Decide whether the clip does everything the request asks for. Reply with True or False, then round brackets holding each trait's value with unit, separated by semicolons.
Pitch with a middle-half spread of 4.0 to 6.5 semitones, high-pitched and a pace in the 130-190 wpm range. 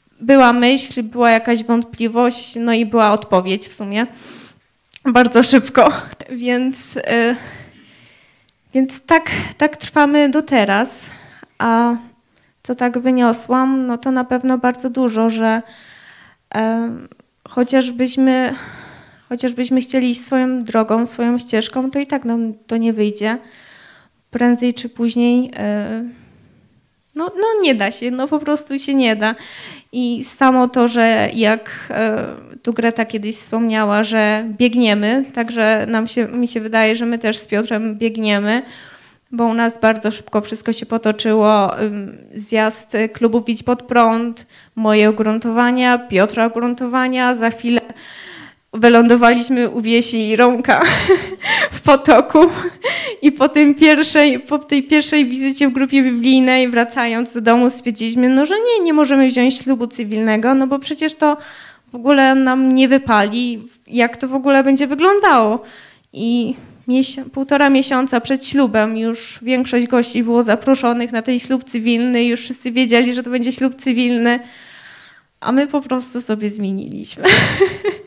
False (2.5 semitones; 245 Hz; 135 wpm)